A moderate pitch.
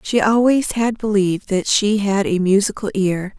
No: high, 205 Hz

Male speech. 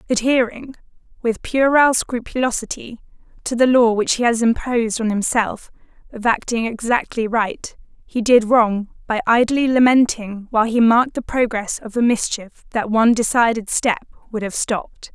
No: female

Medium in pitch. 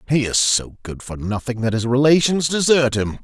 No: low, 125 Hz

